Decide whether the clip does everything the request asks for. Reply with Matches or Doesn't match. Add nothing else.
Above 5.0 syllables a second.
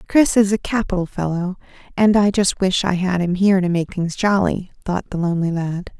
Matches